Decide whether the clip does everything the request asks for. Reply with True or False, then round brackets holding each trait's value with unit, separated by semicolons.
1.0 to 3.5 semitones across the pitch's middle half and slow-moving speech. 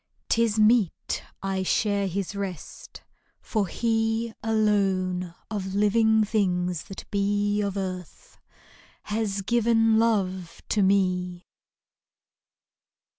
True (2.8 semitones; 100 wpm)